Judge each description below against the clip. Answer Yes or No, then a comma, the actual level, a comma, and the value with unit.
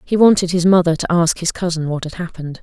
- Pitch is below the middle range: No, medium, 170 Hz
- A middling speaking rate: No, fast, 250 wpm